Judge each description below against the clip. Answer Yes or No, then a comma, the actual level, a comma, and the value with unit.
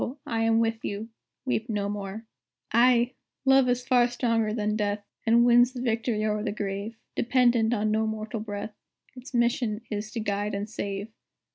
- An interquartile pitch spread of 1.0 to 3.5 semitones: Yes, narrow, 2.4 semitones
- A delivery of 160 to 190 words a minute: Yes, average, 170 wpm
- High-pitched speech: Yes, high, 225 Hz